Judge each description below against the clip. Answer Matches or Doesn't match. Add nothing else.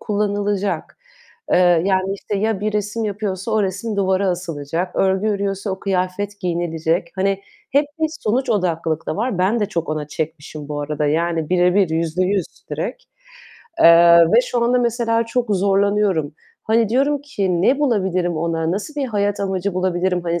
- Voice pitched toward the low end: Doesn't match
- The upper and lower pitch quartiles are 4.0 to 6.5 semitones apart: Doesn't match